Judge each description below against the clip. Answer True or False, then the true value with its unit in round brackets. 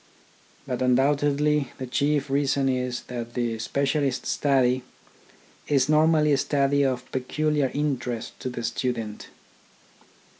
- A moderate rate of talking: False (115 wpm)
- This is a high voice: False (135 Hz)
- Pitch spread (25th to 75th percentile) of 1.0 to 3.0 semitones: True (2.5 semitones)